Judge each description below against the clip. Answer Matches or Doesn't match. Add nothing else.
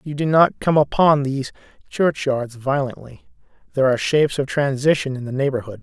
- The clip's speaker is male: Matches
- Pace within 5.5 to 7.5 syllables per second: Matches